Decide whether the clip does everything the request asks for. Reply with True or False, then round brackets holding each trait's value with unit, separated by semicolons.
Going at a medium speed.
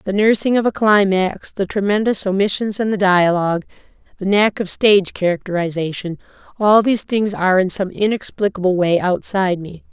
True (150 wpm)